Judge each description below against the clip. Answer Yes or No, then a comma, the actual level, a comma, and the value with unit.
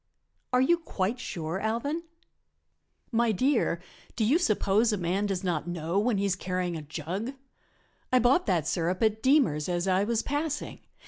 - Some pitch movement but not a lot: No, wide, 5.8 semitones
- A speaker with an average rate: Yes, average, 170 wpm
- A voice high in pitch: Yes, high, 205 Hz